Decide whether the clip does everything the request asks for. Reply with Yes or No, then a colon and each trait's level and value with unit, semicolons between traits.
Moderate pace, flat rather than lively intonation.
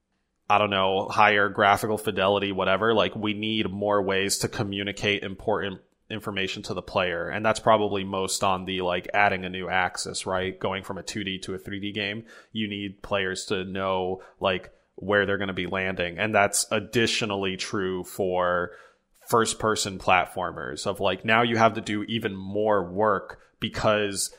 Yes: average, 170 wpm; narrow, 2.1 semitones